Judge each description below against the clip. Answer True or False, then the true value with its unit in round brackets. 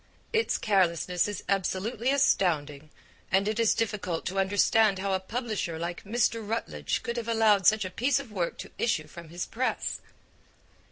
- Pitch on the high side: True (200 Hz)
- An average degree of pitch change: True (4.1 semitones)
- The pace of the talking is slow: False (165 wpm)